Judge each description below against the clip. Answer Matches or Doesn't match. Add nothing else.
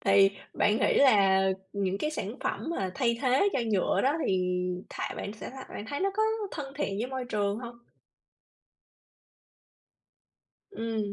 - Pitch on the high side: Matches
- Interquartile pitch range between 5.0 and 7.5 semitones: Matches